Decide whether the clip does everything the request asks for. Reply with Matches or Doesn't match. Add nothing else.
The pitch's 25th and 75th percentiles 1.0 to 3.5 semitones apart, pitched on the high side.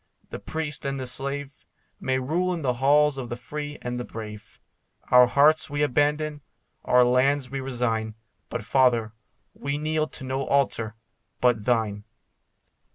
Doesn't match